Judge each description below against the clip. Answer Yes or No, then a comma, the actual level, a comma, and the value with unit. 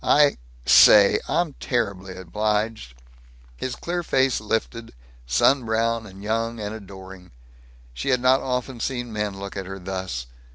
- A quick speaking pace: No, average, 140 wpm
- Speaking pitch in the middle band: No, low, 110 Hz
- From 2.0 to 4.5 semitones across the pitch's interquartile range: Yes, average, 4.2 semitones